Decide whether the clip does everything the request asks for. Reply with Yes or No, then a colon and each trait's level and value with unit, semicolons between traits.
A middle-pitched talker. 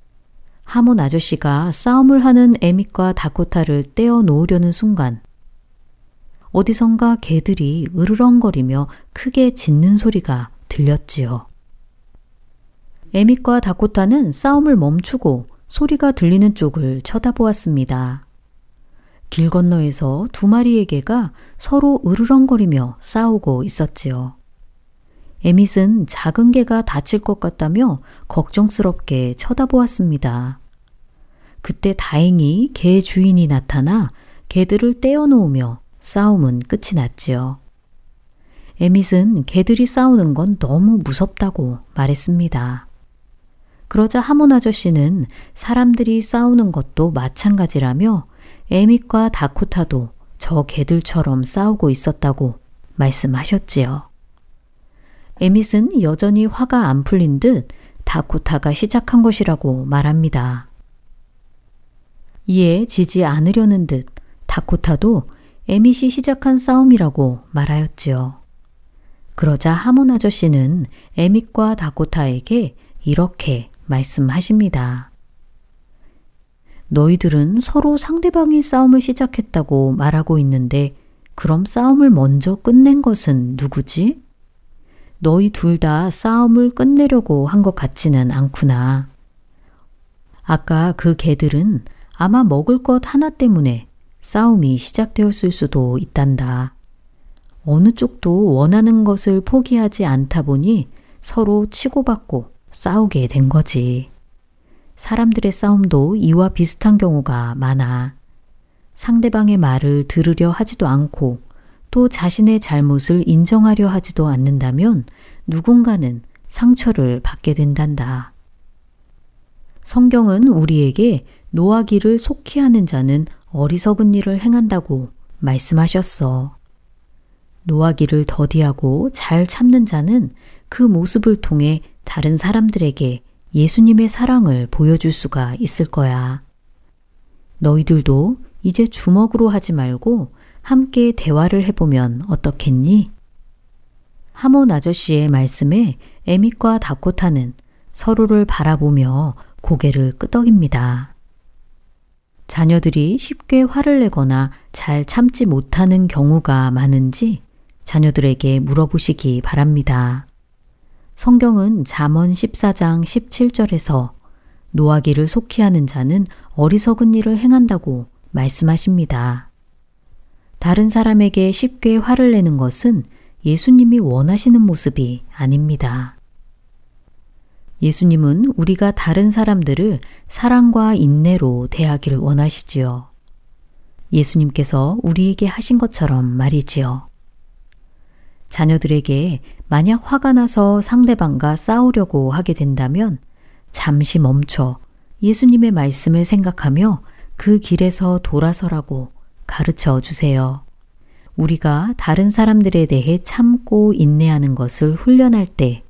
Yes: medium, 165 Hz